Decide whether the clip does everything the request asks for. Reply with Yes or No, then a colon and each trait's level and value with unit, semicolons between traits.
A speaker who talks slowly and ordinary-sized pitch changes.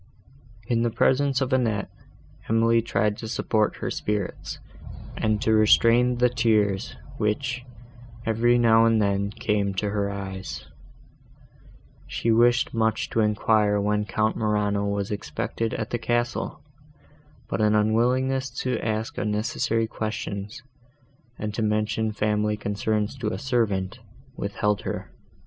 No: slow, 130 wpm; narrow, 1.9 semitones